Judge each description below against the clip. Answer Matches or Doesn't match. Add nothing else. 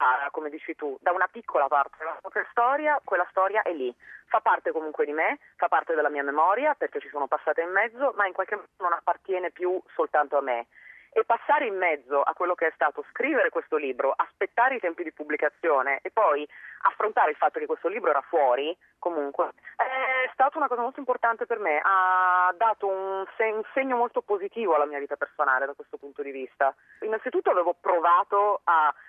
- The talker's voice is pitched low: Doesn't match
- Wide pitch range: Matches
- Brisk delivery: Matches